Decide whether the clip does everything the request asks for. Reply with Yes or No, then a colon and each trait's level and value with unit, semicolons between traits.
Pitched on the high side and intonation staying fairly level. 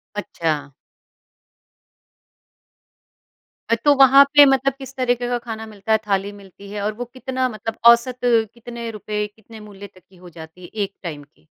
No: high, 220 Hz; average, 4.1 semitones